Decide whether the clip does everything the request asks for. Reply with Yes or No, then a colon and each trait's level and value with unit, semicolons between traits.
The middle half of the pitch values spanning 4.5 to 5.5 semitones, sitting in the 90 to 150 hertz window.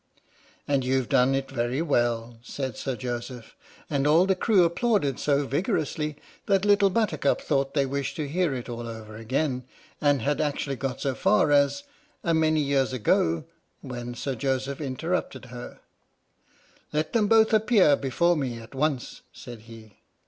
No: average, 4.1 semitones; medium, 140 Hz